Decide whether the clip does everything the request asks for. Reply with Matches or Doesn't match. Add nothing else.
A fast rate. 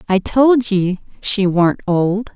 Doesn't match